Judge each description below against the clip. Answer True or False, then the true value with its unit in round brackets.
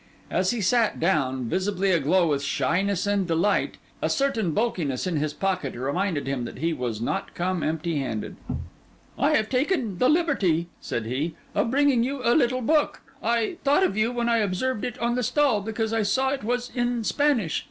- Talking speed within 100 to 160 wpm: False (190 wpm)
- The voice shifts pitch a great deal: True (6.9 semitones)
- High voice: True (200 Hz)